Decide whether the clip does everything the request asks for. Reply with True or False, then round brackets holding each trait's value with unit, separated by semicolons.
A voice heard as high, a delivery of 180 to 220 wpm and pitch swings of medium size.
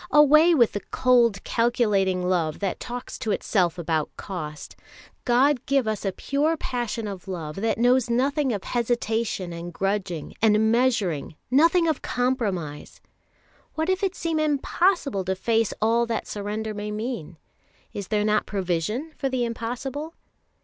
False (225 Hz; 150 wpm; 5.0 semitones)